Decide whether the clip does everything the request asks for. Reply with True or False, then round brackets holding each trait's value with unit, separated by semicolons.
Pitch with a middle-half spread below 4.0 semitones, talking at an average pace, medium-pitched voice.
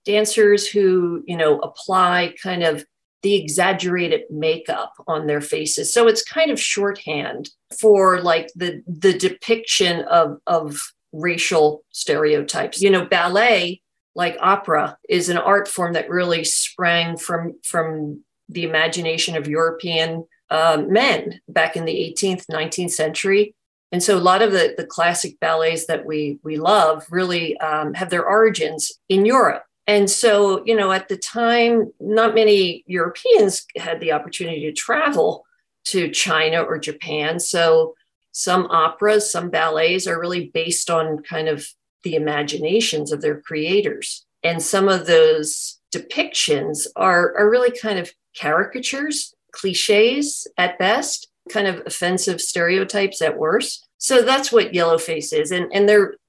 False (4.3 semitones; 145 wpm; 180 Hz)